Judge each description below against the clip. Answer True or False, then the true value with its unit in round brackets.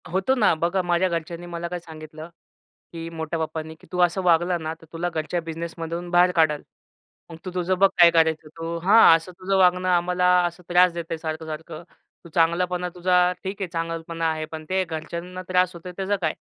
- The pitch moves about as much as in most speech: False (1.8 semitones)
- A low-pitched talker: False (170 Hz)